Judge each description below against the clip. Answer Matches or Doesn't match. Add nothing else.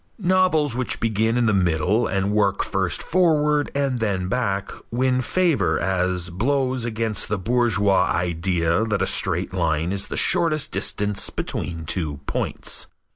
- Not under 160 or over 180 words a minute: Doesn't match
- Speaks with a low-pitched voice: Matches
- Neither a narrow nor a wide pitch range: Doesn't match